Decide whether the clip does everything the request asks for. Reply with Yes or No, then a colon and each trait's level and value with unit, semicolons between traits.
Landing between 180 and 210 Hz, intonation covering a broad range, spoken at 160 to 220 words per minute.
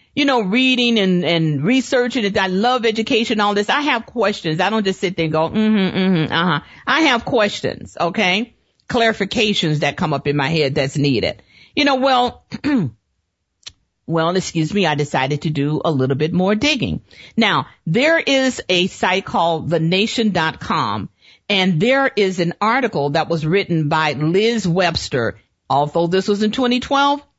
Yes: high, 190 Hz; wide, 6.5 semitones; average, 170 wpm